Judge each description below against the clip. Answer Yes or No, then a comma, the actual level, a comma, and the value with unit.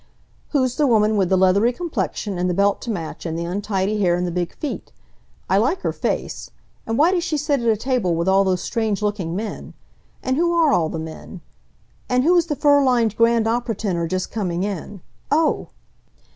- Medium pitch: No, high, 215 Hz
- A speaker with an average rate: No, fast, 210 wpm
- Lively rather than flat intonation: Yes, wide, 5.8 semitones